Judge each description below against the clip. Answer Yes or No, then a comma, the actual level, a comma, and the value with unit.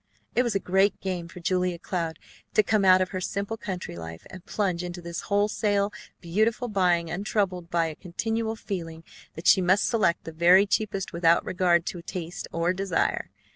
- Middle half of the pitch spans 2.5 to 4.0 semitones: Yes, average, 2.8 semitones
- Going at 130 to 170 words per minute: No, average, 180 wpm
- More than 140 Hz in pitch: Yes, medium, 185 Hz